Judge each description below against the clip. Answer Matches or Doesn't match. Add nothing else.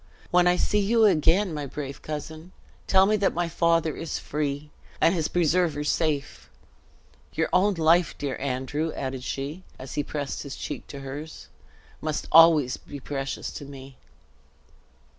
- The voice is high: Doesn't match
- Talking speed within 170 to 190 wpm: Doesn't match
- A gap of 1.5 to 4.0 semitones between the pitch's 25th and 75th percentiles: Matches